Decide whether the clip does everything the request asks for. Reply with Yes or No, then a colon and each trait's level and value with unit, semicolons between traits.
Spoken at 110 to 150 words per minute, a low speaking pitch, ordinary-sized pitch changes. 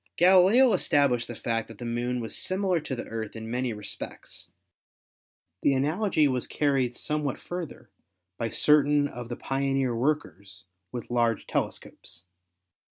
Yes: average, 140 wpm; low, 130 Hz; average, 4.3 semitones